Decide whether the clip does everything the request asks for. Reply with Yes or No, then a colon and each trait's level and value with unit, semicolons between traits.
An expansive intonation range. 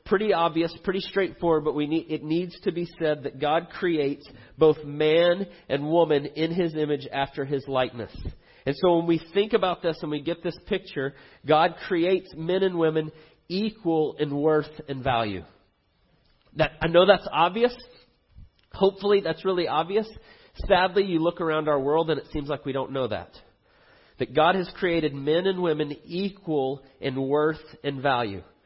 No: average, 3.7 semitones